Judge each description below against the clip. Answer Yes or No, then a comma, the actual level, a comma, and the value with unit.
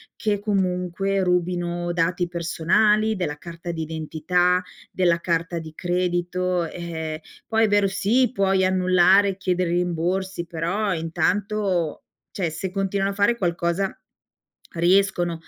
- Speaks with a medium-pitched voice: Yes, medium, 180 Hz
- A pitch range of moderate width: No, narrow, 2.3 semitones